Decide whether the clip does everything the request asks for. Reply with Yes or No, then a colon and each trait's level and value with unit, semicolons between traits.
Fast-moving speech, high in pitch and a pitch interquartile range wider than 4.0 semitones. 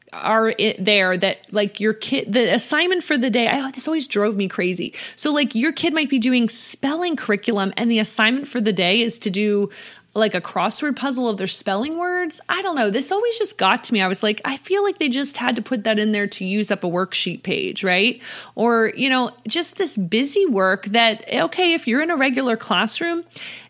Yes: fast, 230 wpm; high, 230 Hz; average, 5.2 semitones